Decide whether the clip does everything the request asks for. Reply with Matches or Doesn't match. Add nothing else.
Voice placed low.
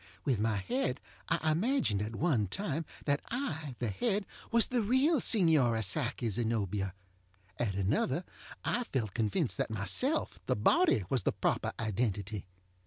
Matches